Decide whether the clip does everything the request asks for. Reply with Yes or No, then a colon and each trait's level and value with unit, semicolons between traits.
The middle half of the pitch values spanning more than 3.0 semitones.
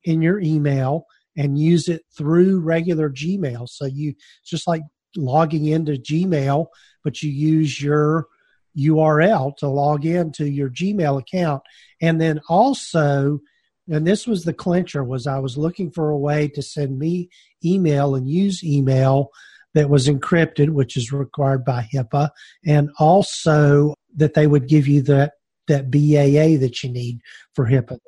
No: average, 2.7 semitones